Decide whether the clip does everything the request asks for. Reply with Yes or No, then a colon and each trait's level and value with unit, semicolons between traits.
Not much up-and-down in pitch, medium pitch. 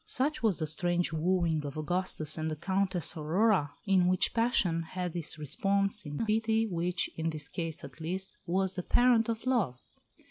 No: average, 3.9 semitones; medium, 180 Hz